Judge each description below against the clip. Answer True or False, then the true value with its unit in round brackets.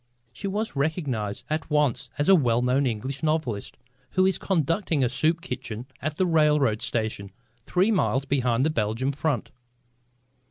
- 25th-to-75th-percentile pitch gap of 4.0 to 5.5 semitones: True (4.8 semitones)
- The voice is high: False (140 Hz)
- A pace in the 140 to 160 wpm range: True (155 wpm)